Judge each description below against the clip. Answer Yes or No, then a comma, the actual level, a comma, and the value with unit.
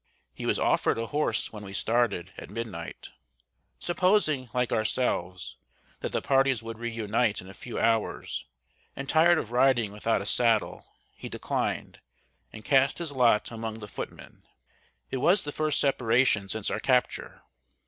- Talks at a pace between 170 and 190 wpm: No, average, 160 wpm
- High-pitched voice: No, low, 115 Hz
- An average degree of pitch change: Yes, average, 3.7 semitones